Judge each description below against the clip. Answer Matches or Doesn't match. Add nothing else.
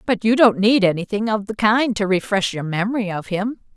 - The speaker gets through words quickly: Matches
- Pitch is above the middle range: Matches